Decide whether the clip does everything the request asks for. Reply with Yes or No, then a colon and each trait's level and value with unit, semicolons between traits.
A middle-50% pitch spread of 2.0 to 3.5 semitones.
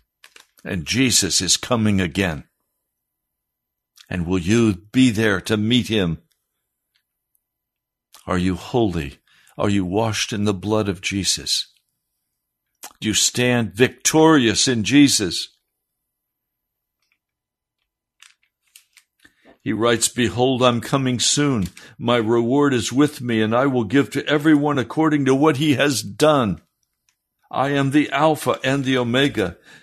No: average, 5.0 semitones